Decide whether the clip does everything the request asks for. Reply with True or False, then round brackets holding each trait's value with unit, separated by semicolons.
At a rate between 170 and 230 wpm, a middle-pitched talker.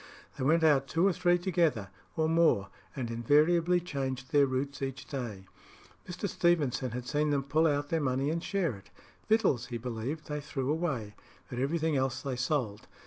True (180 wpm; 145 Hz)